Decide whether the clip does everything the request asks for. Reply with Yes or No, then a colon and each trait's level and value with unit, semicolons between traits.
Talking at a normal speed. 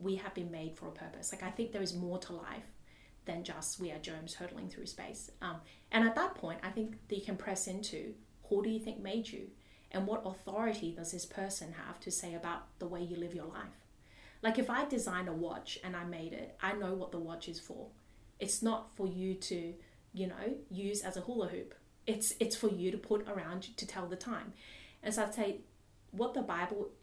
No: fast, 230 wpm